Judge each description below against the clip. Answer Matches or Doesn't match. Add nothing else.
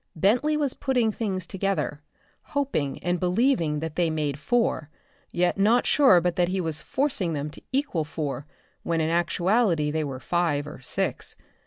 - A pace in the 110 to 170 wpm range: Matches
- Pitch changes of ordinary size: Doesn't match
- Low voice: Doesn't match